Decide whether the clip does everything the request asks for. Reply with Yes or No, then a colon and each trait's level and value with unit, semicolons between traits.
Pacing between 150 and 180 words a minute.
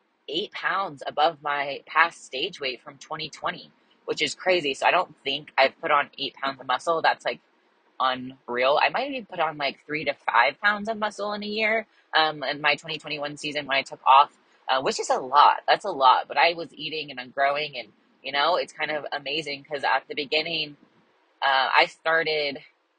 No: fast, 205 wpm